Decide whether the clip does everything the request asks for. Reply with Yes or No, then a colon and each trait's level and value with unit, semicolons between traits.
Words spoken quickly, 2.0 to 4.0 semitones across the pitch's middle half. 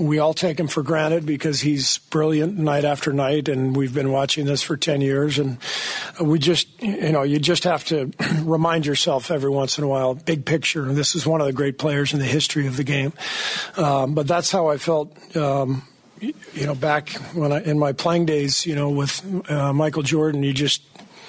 Yes: fast, 215 wpm; narrow, 2.5 semitones